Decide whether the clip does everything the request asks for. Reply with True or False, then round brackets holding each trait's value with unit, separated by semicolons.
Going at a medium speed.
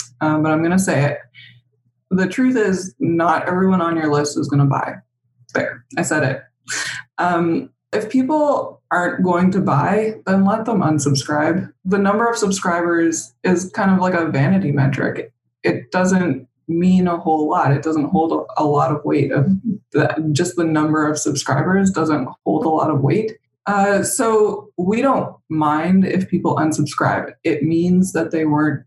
True (175 wpm)